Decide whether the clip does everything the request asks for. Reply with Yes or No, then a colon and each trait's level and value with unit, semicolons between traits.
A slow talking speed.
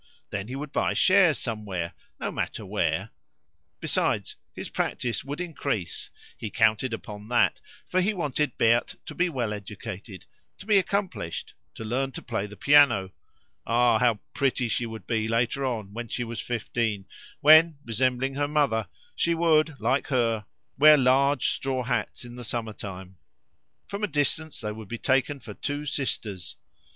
No: average, 165 wpm